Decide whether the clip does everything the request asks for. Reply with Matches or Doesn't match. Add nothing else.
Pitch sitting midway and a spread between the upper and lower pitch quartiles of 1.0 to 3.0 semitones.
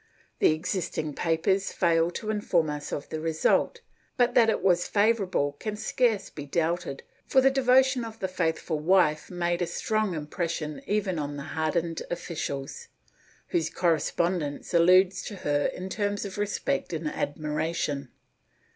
Doesn't match